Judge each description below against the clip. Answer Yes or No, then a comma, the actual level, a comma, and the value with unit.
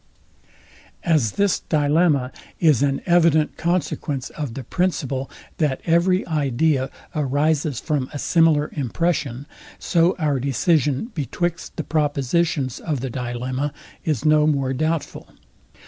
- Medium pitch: Yes, medium, 150 Hz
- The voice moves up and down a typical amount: Yes, average, 3.4 semitones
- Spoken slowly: Yes, slow, 115 wpm